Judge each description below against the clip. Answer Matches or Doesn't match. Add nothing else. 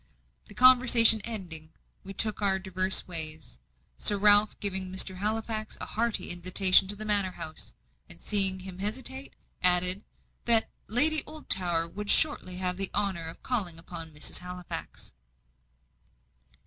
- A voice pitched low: Doesn't match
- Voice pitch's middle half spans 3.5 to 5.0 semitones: Doesn't match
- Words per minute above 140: Doesn't match